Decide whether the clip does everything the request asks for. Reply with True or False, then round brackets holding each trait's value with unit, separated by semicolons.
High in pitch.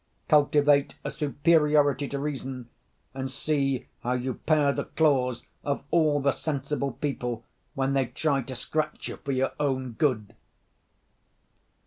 False (140 Hz)